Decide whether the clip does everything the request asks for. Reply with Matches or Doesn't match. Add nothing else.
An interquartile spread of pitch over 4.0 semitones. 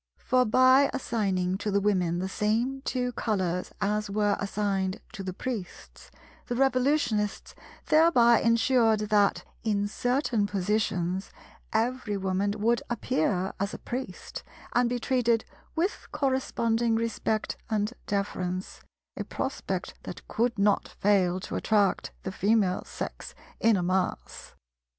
Doesn't match